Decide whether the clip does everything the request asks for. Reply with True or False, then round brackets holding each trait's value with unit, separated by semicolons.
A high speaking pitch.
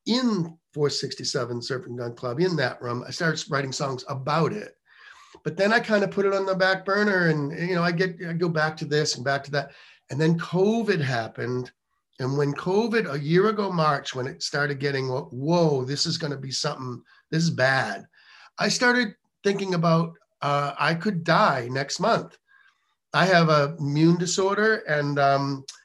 False (160 Hz)